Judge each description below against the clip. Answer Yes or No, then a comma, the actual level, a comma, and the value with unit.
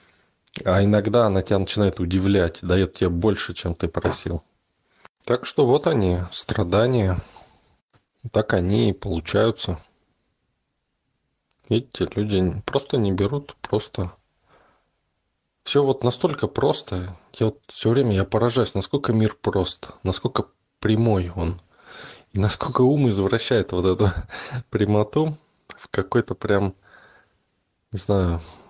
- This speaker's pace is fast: No, average, 115 wpm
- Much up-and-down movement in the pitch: No, average, 3.7 semitones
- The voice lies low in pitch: Yes, low, 100 Hz